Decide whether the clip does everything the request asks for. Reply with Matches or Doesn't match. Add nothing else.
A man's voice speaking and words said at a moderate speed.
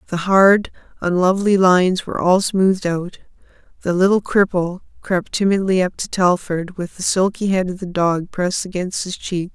Doesn't match